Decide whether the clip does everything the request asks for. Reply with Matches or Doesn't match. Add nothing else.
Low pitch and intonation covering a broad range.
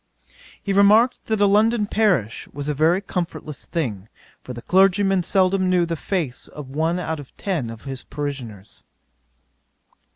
Doesn't match